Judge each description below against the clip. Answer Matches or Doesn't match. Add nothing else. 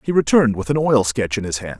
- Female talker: Doesn't match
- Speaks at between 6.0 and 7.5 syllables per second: Matches